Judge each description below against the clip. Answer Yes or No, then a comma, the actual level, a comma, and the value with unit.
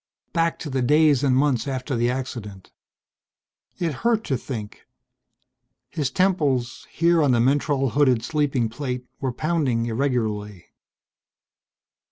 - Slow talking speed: Yes, slow, 125 wpm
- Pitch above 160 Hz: No, low, 135 Hz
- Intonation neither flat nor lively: Yes, average, 3.7 semitones